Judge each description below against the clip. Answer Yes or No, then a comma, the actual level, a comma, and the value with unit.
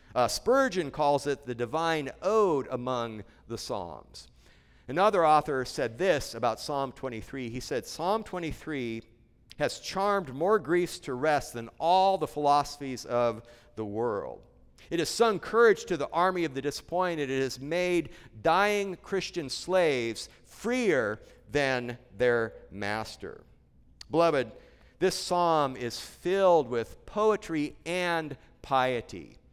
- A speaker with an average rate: No, slow, 130 wpm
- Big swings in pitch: Yes, wide, 6.7 semitones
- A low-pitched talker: No, medium, 145 Hz